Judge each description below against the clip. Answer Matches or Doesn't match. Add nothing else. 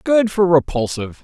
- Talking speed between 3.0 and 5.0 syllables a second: Doesn't match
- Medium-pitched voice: Matches